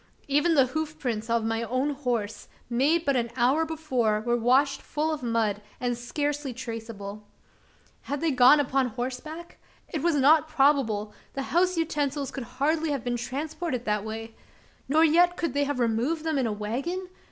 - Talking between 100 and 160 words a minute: No, average, 175 wpm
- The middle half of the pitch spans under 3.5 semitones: No, average, 4.8 semitones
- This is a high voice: Yes, very high, 270 Hz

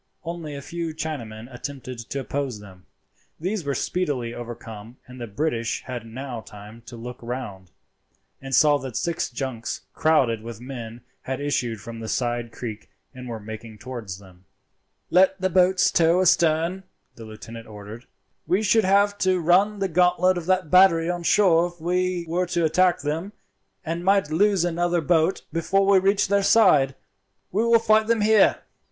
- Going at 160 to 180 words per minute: Yes, average, 170 wpm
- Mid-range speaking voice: Yes, medium, 155 Hz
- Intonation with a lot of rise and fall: Yes, wide, 7.5 semitones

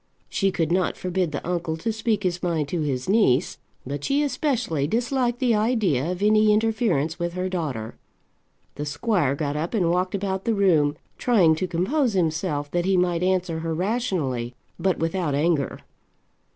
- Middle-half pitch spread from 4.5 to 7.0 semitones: Yes, average, 5.1 semitones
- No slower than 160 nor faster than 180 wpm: Yes, average, 170 wpm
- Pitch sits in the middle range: Yes, medium, 180 Hz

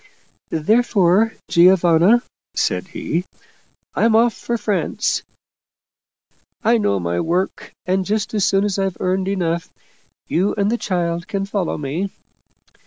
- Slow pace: Yes, slow, 130 wpm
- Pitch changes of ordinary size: Yes, average, 3.5 semitones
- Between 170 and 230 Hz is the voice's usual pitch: Yes, high, 190 Hz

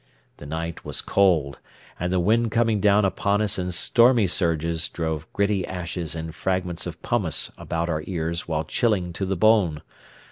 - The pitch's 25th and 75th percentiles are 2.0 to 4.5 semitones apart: Yes, average, 3.6 semitones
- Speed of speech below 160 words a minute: No, average, 170 wpm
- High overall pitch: No, very low, 90 Hz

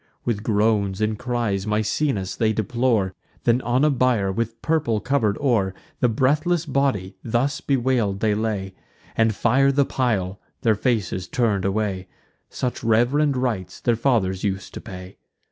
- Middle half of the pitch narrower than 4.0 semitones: No, average, 4.4 semitones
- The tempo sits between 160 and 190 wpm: No, average, 145 wpm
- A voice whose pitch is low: Yes, low, 110 Hz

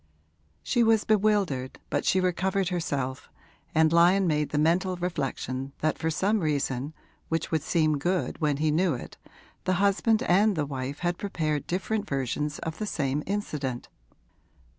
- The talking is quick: No, average, 155 wpm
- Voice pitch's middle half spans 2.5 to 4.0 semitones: No, average, 4.5 semitones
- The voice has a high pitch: No, medium, 165 Hz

